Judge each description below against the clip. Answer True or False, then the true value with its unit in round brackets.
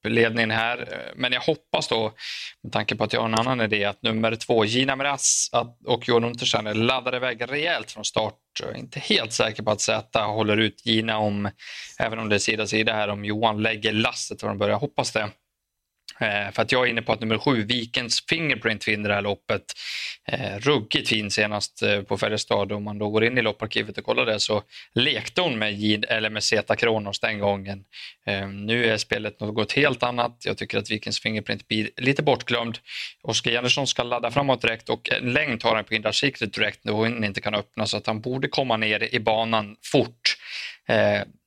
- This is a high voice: False (110 Hz)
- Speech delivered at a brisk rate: True (205 wpm)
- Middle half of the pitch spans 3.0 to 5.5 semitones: False (2.4 semitones)